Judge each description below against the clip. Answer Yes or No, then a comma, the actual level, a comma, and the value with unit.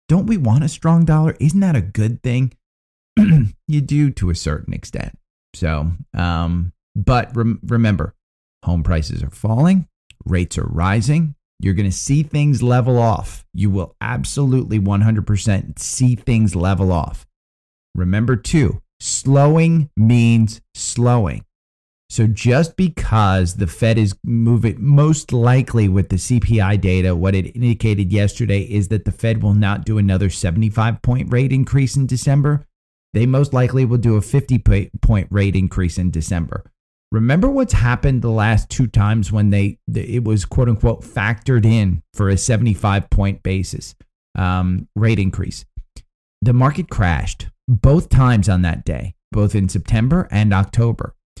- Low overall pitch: Yes, low, 110 Hz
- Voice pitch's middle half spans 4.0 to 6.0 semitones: Yes, average, 4.6 semitones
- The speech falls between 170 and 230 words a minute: No, average, 150 wpm